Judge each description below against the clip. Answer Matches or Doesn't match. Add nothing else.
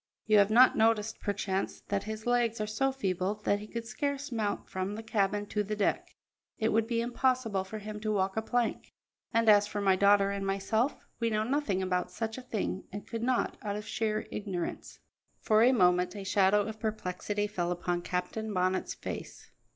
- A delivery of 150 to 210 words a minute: Matches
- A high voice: Matches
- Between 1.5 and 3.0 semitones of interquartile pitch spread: Matches